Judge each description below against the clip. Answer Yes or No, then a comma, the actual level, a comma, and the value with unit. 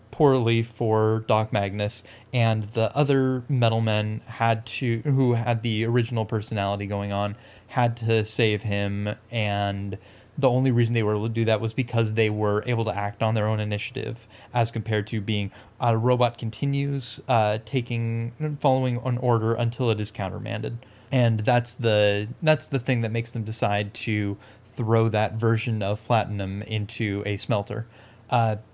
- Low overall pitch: Yes, low, 115 Hz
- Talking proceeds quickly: No, average, 165 wpm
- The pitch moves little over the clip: Yes, narrow, 2.1 semitones